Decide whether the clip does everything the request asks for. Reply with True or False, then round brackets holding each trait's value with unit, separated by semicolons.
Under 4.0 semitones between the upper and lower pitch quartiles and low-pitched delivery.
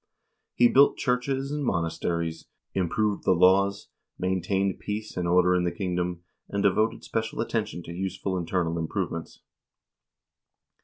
True (3.6 semitones; 95 Hz)